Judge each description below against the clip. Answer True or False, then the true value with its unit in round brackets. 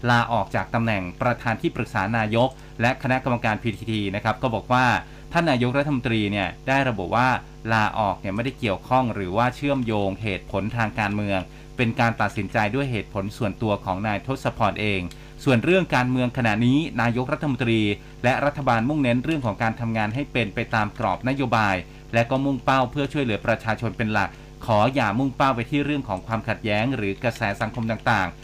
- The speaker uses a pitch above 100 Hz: True (115 Hz)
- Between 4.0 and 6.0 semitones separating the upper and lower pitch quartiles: False (3.6 semitones)